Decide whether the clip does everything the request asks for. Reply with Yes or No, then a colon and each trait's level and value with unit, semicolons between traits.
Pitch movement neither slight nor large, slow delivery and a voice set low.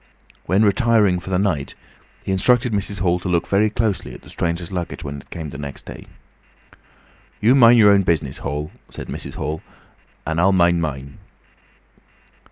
No: average, 4.5 semitones; average, 170 wpm; very low, 90 Hz